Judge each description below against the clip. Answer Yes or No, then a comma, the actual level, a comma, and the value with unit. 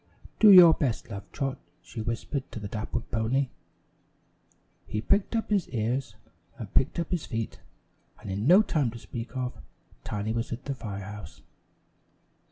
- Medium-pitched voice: No, low, 120 Hz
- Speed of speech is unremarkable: Yes, average, 165 wpm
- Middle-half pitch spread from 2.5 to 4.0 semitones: No, average, 4.4 semitones